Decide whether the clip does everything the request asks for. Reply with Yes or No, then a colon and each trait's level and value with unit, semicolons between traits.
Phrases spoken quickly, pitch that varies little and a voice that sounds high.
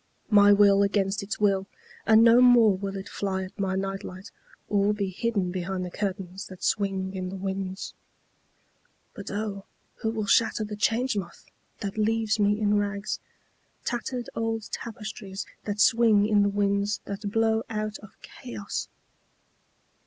No: average, 150 wpm; narrow, 2.0 semitones; high, 205 Hz